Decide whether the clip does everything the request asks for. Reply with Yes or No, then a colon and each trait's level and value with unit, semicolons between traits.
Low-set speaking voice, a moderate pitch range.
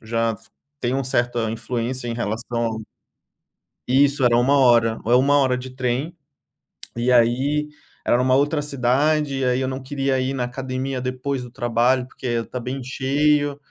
No: low, 130 Hz; narrow, 2.1 semitones